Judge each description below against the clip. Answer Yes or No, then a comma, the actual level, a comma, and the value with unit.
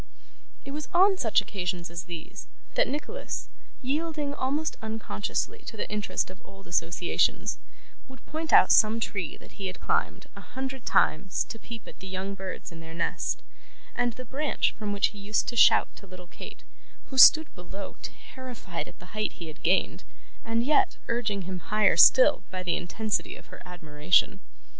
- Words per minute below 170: No, average, 175 wpm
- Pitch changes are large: Yes, wide, 6.2 semitones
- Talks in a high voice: Yes, high, 210 Hz